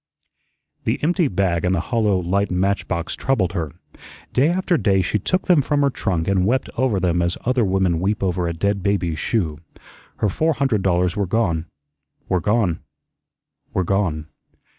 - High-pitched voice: No, very low, 95 Hz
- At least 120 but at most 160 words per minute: No, average, 175 wpm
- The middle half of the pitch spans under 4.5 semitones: No, average, 4.8 semitones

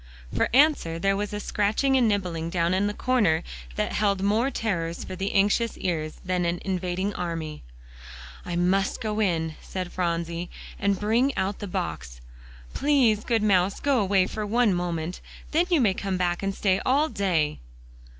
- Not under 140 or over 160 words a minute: No, average, 170 wpm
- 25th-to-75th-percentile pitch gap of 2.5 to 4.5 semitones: Yes, average, 3.4 semitones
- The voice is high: Yes, high, 195 Hz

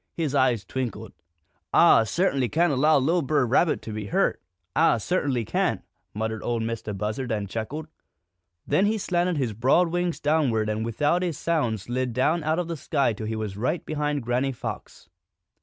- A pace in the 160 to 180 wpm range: Yes, average, 175 wpm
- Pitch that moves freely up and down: Yes, wide, 5.9 semitones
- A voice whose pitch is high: No, low, 130 Hz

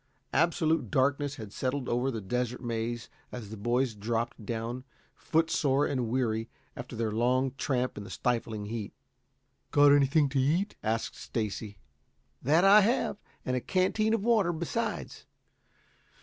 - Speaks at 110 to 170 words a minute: Yes, average, 145 wpm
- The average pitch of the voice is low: Yes, low, 130 Hz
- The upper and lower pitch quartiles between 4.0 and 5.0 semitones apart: Yes, average, 4.4 semitones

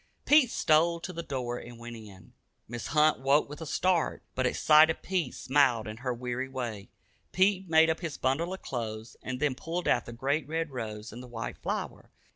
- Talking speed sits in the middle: No, fast, 210 wpm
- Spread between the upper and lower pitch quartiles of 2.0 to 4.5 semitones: No, average, 5.2 semitones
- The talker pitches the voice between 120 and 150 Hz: Yes, low, 135 Hz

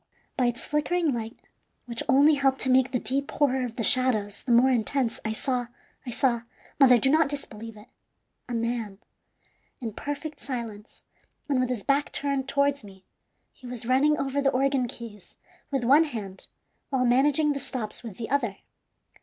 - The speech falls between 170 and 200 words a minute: Yes, average, 175 wpm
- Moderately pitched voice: No, very high, 255 Hz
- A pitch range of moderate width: Yes, average, 3.2 semitones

